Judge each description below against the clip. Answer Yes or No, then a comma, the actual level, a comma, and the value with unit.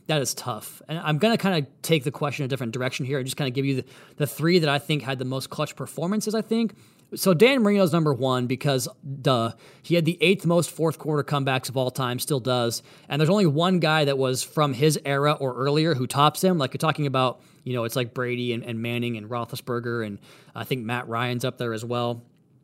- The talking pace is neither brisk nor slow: No, fast, 245 wpm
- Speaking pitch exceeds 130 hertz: Yes, medium, 140 Hz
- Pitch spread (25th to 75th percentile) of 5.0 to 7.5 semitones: No, average, 3.6 semitones